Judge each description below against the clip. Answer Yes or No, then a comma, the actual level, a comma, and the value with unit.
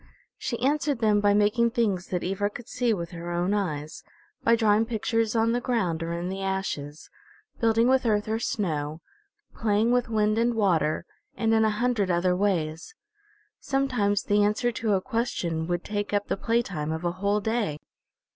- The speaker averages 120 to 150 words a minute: No, average, 180 wpm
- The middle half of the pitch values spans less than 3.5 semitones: No, average, 4.4 semitones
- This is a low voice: No, high, 205 Hz